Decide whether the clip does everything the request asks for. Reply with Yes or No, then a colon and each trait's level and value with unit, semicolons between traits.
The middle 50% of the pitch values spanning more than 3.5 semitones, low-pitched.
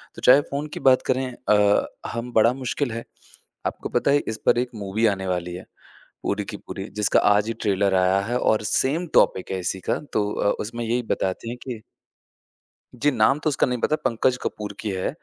Yes: average, 4.0 semitones; low, 115 Hz